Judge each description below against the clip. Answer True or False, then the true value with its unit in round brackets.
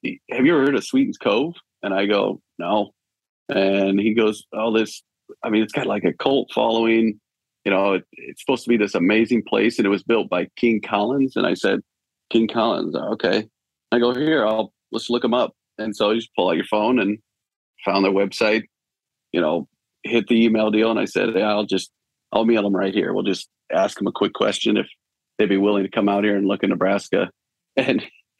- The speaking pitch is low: True (110 Hz)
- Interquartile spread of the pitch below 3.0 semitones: True (2.5 semitones)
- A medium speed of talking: False (220 wpm)